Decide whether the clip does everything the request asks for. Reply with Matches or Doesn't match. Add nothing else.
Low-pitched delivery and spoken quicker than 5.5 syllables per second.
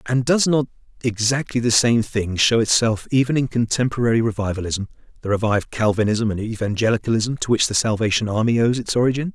Matches